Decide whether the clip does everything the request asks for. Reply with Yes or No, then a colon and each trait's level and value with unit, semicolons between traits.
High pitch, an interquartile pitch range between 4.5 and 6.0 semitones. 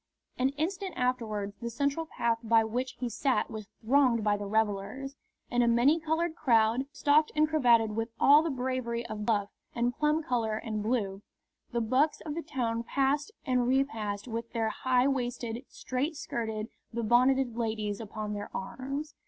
No: high, 240 Hz; average, 3.6 semitones